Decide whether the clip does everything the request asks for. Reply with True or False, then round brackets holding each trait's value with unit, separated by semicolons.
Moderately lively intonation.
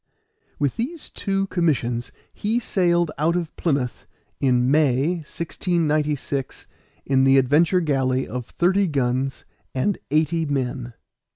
True (4.6 semitones)